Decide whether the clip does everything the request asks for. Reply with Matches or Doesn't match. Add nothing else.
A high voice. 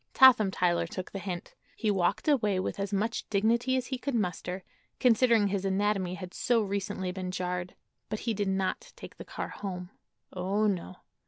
Matches